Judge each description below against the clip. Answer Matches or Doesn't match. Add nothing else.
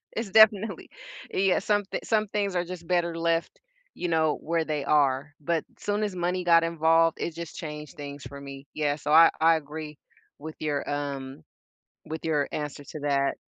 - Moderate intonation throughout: Matches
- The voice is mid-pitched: Matches